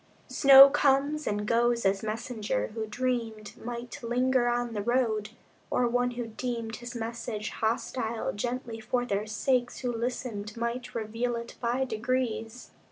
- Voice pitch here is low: No, high, 235 Hz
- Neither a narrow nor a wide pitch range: No, narrow, 2.1 semitones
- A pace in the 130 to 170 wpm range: Yes, average, 145 wpm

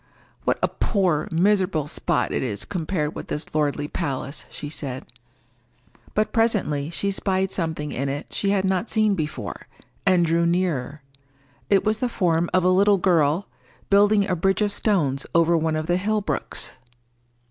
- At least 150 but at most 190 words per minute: Yes, average, 165 wpm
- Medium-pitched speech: Yes, medium, 175 Hz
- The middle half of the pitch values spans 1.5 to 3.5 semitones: No, average, 4.6 semitones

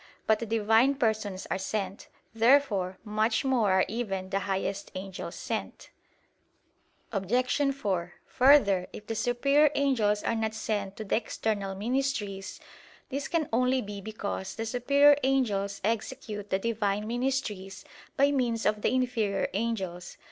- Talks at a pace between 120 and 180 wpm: Yes, average, 140 wpm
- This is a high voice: Yes, high, 220 Hz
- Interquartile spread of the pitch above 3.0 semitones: Yes, average, 4.1 semitones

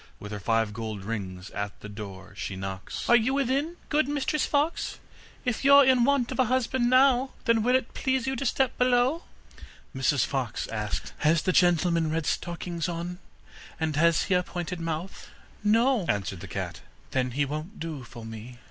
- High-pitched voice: No, medium, 170 Hz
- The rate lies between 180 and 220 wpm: Yes, average, 185 wpm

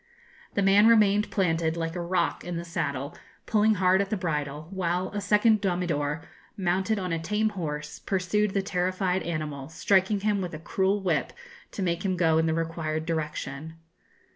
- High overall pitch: No, medium, 180 Hz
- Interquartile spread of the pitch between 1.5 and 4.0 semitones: Yes, average, 3.5 semitones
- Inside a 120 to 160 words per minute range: No, average, 175 wpm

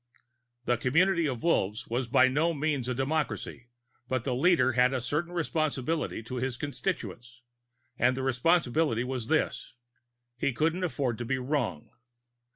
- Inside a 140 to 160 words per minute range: Yes, average, 150 wpm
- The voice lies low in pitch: Yes, low, 130 Hz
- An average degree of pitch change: Yes, average, 4.3 semitones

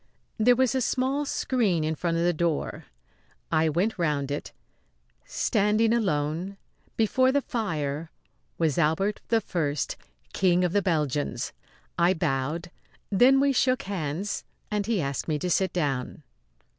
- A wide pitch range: Yes, wide, 6.1 semitones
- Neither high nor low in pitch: Yes, medium, 175 Hz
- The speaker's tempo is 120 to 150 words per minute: Yes, average, 140 wpm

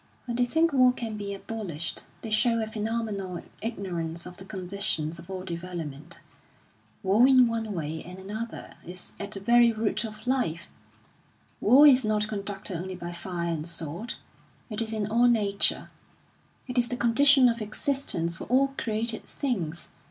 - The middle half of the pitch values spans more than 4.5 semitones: Yes, average, 4.9 semitones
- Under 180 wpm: Yes, average, 165 wpm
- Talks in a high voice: Yes, high, 210 Hz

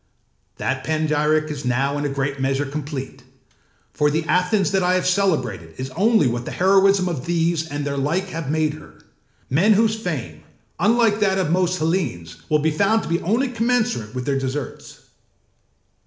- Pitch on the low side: No, medium, 155 Hz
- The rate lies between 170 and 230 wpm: Yes, average, 175 wpm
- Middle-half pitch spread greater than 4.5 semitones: Yes, wide, 5.5 semitones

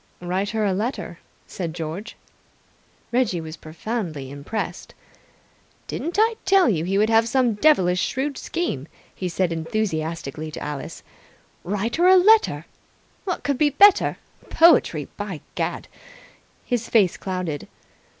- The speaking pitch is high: Yes, high, 205 Hz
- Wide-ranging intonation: Yes, wide, 7.7 semitones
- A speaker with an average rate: No, slow, 130 wpm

